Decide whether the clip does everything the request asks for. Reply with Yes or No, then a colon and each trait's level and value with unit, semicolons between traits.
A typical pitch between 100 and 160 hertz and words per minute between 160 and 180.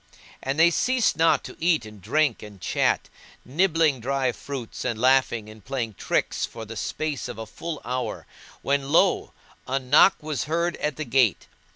Yes: low, 135 Hz; average, 175 wpm